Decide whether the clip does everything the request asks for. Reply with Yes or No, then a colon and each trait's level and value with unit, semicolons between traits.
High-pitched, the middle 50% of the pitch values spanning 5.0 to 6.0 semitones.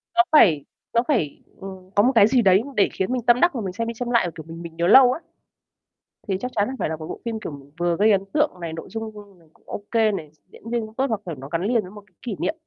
Yes: high, 205 Hz; average, 5.3 semitones